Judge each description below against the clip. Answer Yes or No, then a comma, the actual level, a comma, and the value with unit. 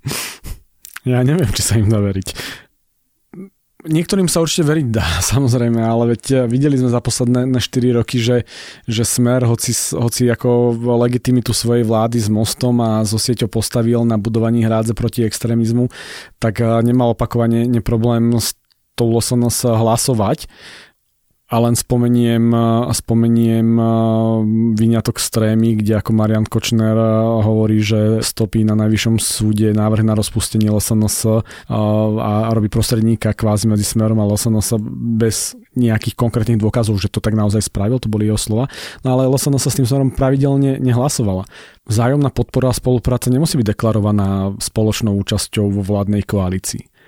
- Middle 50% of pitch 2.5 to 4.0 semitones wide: No, narrow, 2.0 semitones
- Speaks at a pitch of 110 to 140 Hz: Yes, low, 115 Hz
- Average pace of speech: Yes, average, 140 wpm